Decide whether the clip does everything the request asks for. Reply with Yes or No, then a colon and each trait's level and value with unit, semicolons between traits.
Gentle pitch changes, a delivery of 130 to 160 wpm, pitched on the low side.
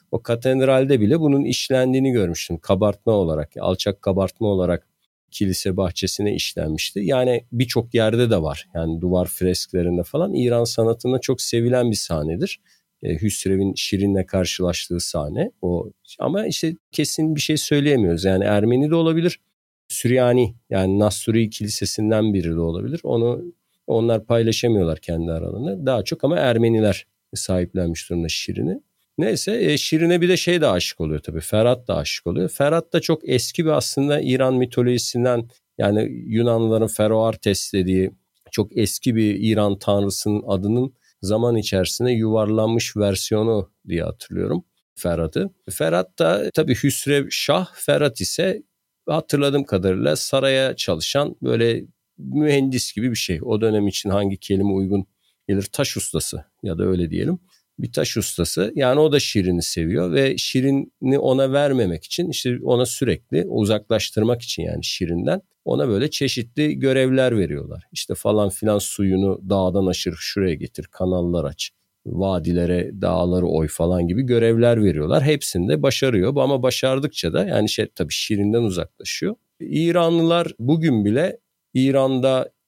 No: wide, 5.6 semitones; average, 135 wpm; low, 110 Hz